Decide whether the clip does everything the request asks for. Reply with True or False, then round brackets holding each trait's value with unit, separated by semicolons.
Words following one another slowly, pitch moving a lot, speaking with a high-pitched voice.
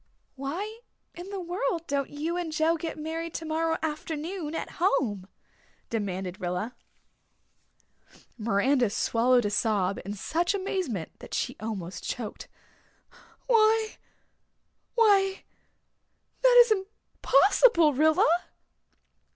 True (100 wpm; 8.6 semitones; 315 Hz)